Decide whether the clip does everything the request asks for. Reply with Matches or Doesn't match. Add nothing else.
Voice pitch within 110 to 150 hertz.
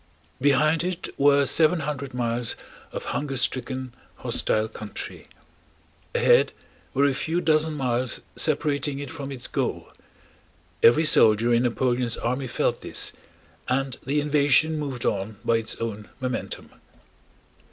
Matches